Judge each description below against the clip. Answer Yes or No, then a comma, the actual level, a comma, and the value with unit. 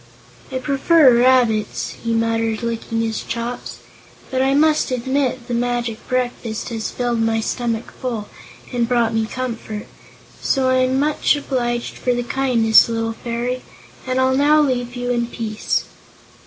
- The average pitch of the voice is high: Yes, high, 245 Hz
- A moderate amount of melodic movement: No, narrow, 2.2 semitones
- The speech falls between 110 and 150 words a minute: Yes, average, 145 wpm